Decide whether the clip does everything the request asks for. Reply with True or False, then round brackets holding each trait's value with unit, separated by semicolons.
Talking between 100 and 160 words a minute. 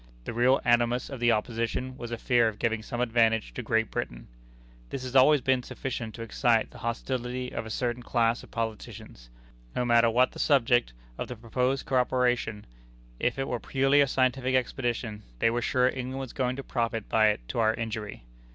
False (195 wpm)